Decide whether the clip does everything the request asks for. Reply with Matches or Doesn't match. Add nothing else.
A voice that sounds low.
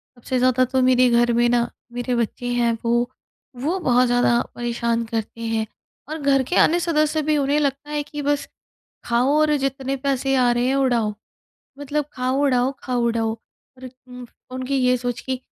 Doesn't match